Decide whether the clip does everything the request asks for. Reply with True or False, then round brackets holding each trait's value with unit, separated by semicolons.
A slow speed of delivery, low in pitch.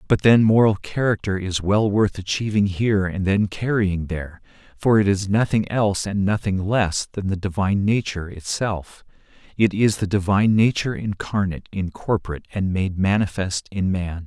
False (160 wpm; 100 Hz)